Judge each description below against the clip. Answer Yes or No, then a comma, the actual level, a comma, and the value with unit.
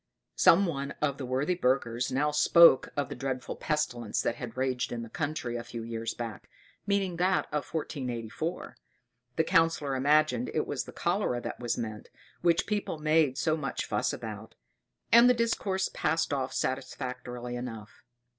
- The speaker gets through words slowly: No, average, 165 wpm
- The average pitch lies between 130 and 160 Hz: Yes, low, 135 Hz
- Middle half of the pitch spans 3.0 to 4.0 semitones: No, average, 4.9 semitones